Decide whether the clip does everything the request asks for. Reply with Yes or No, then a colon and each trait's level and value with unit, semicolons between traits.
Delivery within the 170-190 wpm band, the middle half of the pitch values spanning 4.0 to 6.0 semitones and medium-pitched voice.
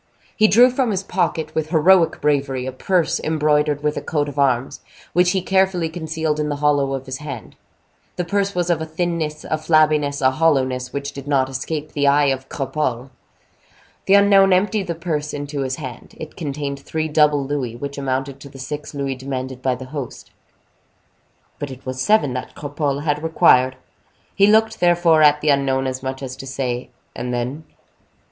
No: average, 185 wpm; average, 3.2 semitones; medium, 145 Hz